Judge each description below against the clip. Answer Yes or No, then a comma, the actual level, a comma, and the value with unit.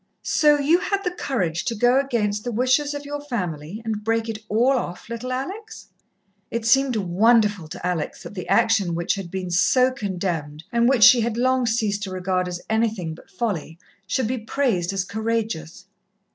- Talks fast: No, average, 185 wpm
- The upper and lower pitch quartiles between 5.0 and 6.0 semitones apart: Yes, wide, 5.6 semitones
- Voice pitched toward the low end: No, high, 220 Hz